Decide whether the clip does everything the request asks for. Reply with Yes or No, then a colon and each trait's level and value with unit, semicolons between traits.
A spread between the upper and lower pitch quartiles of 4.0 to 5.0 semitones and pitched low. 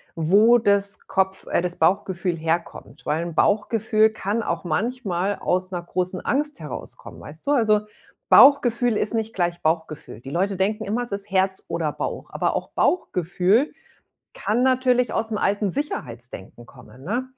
No: average, 4.6 semitones; high, 195 Hz